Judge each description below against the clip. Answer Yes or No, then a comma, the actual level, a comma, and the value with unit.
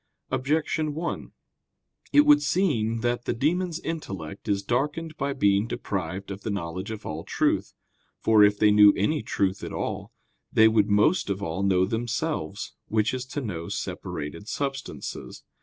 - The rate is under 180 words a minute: Yes, average, 155 wpm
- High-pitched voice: No, low, 110 Hz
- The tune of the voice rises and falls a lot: Yes, wide, 6.6 semitones